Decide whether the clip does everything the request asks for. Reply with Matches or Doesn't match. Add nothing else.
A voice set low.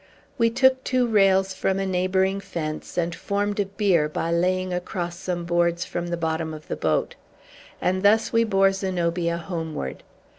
Doesn't match